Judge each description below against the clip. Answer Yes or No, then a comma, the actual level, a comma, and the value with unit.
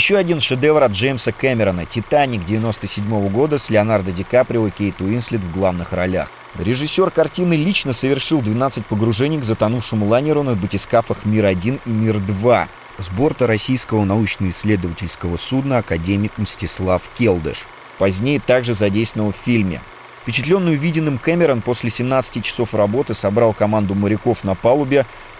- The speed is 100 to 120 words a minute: No, average, 135 wpm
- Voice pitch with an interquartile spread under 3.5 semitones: No, average, 4.3 semitones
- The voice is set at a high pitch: No, low, 115 Hz